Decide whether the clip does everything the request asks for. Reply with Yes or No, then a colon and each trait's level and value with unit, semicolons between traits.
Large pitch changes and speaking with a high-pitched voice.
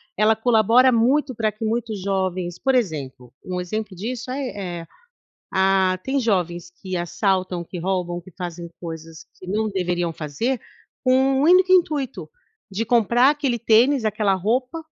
Yes: wide, 5.7 semitones; high, 210 Hz